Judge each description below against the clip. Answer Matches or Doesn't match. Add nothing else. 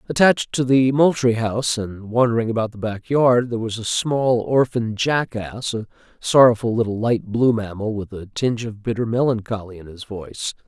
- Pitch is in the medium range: Doesn't match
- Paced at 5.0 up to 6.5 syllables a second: Matches